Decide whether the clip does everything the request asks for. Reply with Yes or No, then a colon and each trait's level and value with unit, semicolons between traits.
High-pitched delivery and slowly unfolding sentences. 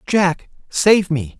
No: medium, 175 Hz; slow, 130 wpm